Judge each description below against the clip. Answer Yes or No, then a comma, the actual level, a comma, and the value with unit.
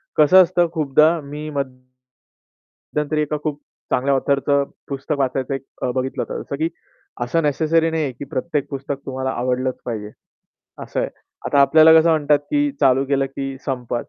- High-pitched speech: No, medium, 140 Hz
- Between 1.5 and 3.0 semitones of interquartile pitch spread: Yes, average, 2.7 semitones